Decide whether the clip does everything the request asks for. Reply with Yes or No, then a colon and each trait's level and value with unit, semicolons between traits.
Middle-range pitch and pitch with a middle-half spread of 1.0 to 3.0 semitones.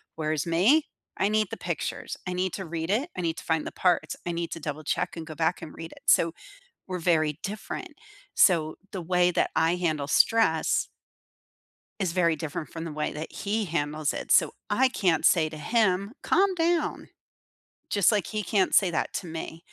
No: medium, 170 Hz; average, 3.6 semitones